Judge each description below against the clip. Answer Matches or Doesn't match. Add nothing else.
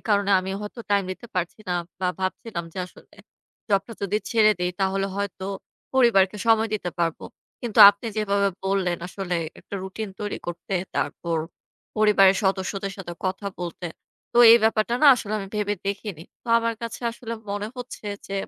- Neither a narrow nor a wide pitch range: Doesn't match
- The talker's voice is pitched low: Doesn't match